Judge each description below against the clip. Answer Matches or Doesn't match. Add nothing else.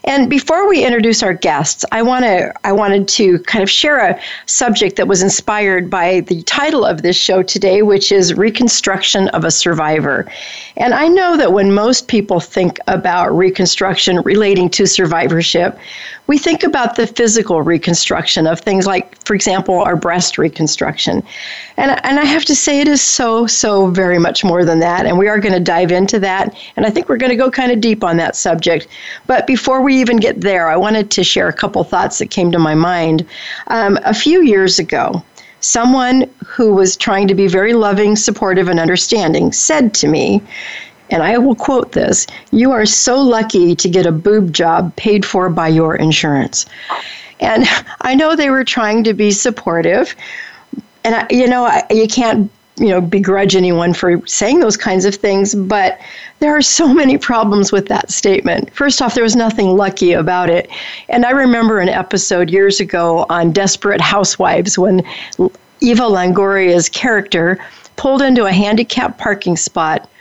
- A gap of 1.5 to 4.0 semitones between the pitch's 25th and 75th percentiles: Doesn't match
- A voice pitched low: Doesn't match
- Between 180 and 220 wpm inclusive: Matches